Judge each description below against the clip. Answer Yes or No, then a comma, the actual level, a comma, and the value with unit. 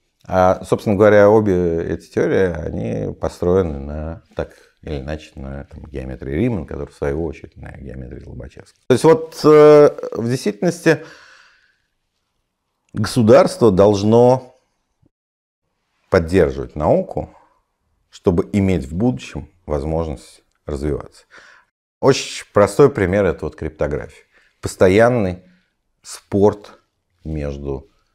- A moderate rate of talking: No, slow, 100 wpm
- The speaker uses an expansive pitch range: Yes, wide, 8.2 semitones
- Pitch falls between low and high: No, very low, 95 Hz